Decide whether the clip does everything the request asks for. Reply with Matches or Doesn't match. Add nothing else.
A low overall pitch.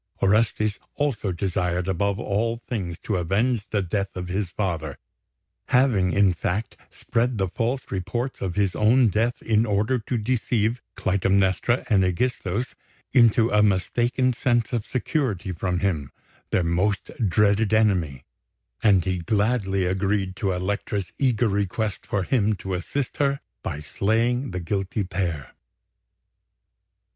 Matches